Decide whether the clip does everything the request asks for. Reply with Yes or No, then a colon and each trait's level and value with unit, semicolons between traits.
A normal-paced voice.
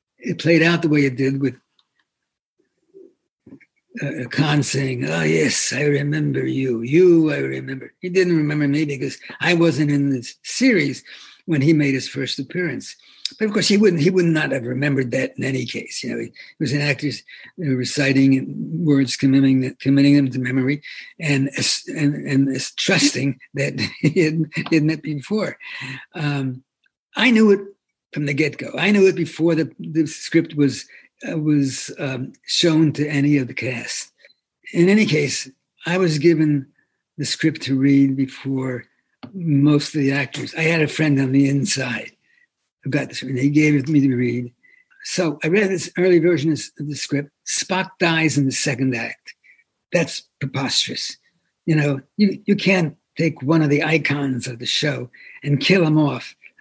Yes: average, 175 wpm